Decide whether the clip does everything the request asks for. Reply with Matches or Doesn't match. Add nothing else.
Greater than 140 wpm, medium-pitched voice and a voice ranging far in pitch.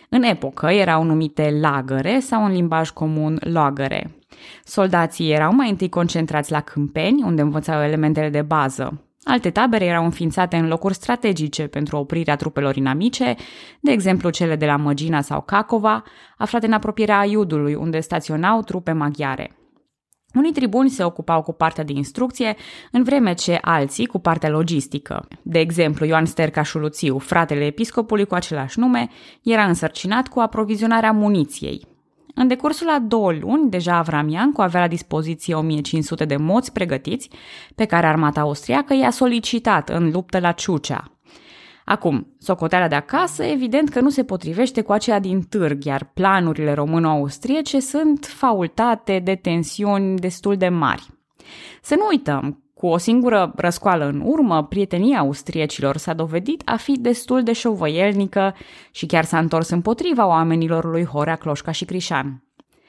Matches